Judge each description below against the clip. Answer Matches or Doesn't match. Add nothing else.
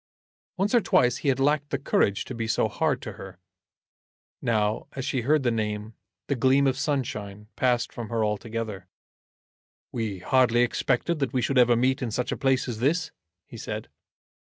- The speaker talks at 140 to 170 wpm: Doesn't match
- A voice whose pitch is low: Matches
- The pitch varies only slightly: Doesn't match